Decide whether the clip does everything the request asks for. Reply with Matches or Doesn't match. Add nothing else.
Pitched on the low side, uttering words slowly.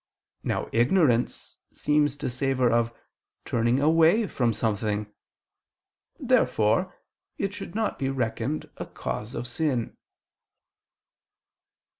Matches